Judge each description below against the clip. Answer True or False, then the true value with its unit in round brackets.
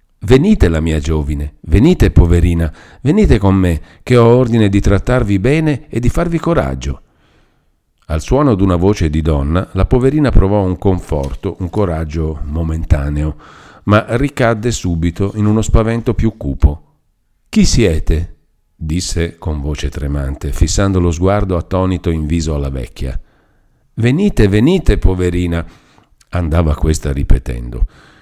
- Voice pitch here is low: True (90 Hz)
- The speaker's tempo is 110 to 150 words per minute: True (130 wpm)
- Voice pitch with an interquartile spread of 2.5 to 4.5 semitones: False (5.3 semitones)